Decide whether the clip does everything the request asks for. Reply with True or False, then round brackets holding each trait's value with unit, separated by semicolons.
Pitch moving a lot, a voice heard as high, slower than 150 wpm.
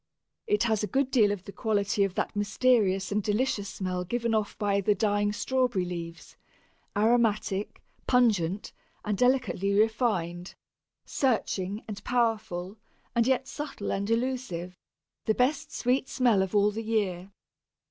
False (3.7 semitones; 210 Hz; 140 wpm)